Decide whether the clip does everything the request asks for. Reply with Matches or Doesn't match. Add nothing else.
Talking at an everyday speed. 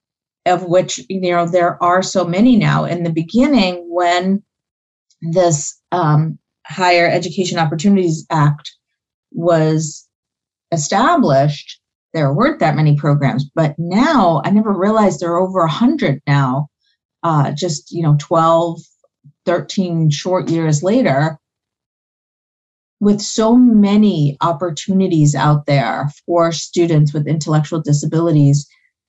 Doesn't match